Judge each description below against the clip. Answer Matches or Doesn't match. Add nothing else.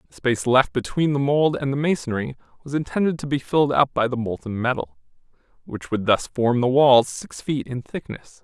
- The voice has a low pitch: Matches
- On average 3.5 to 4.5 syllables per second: Doesn't match